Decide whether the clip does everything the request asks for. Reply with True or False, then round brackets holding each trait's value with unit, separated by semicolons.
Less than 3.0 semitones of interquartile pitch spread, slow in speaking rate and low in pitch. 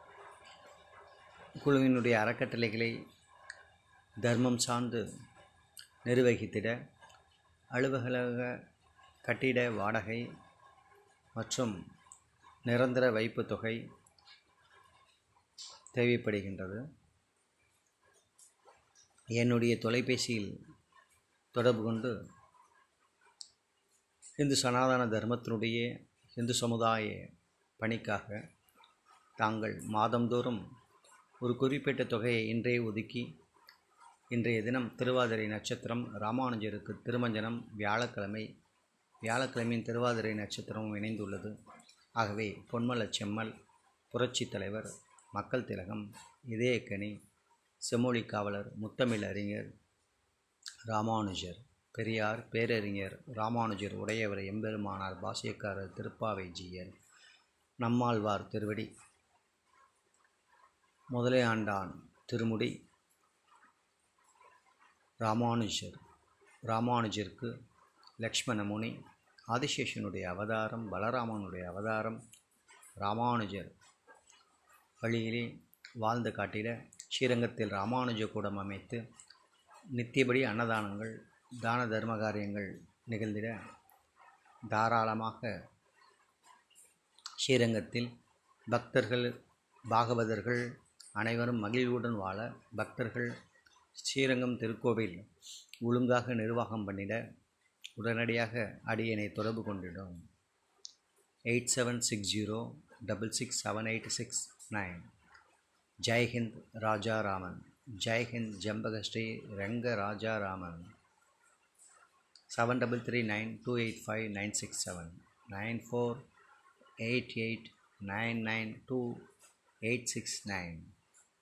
True (2.4 semitones; 70 wpm; 115 Hz)